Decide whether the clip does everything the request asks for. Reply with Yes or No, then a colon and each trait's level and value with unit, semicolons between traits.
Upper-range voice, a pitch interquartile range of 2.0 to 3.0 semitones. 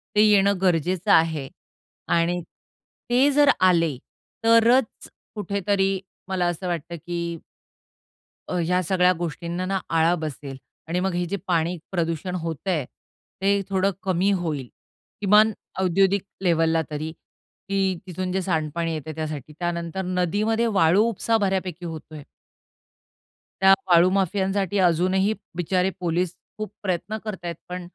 No: medium, 180 Hz; average, 2.7 semitones